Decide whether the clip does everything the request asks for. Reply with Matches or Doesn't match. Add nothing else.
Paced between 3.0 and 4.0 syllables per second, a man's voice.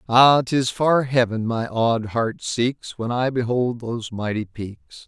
Matches